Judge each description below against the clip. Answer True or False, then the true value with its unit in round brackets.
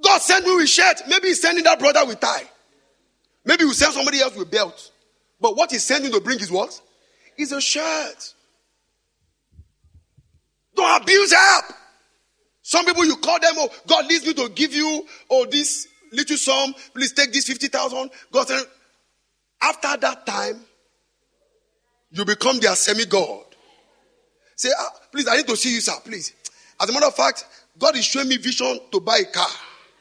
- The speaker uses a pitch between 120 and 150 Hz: False (295 Hz)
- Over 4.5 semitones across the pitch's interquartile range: True (5.0 semitones)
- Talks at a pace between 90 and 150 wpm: False (170 wpm)